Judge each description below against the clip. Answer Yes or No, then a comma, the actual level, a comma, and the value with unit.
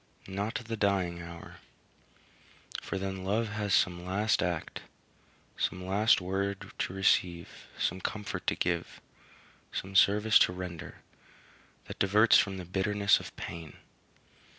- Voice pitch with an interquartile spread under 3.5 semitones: Yes, narrow, 2.4 semitones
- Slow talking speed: Yes, slow, 130 wpm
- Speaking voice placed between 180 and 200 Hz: No, very low, 95 Hz